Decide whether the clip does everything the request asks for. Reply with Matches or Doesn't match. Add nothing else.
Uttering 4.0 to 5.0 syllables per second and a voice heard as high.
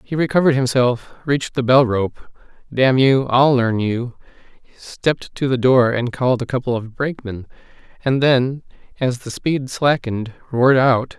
Doesn't match